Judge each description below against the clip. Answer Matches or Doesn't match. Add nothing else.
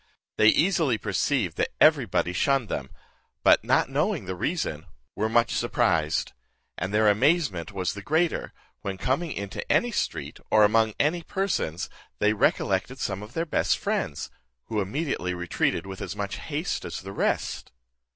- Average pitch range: Doesn't match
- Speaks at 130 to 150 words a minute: Doesn't match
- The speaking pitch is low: Matches